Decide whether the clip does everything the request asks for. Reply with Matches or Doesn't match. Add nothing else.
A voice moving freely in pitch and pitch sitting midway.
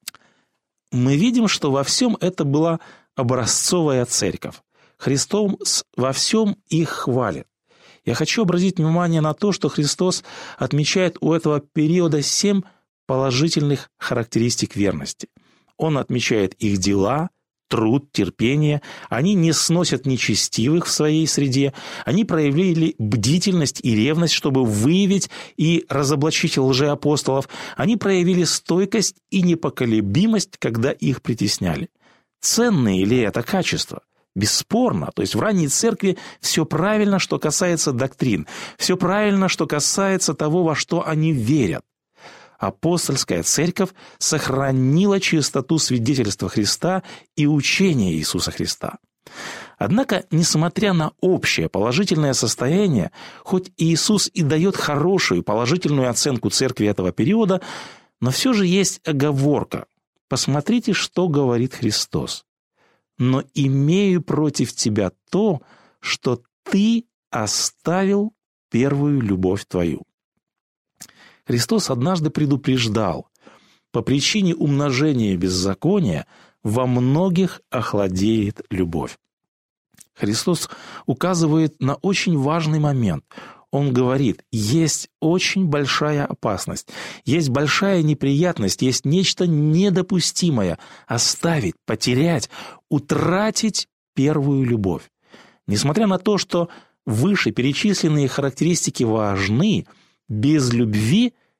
Matches